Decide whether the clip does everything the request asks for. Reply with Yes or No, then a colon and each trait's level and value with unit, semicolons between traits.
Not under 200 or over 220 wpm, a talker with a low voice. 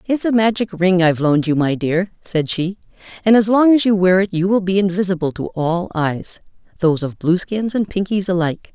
No: fast, 205 wpm; medium, 185 Hz